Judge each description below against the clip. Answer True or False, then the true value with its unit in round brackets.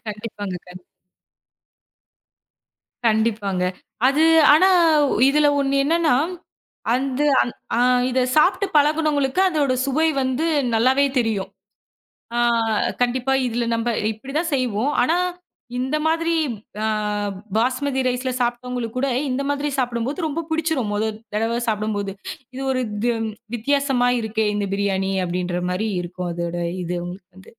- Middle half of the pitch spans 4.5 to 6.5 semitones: True (4.9 semitones)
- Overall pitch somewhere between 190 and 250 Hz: True (245 Hz)